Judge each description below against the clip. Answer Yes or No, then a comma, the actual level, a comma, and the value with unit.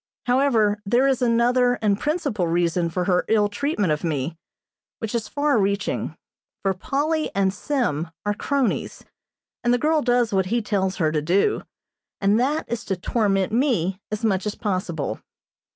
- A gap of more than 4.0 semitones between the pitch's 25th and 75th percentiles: Yes, average, 4.7 semitones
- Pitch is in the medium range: No, high, 210 Hz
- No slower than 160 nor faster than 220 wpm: Yes, average, 165 wpm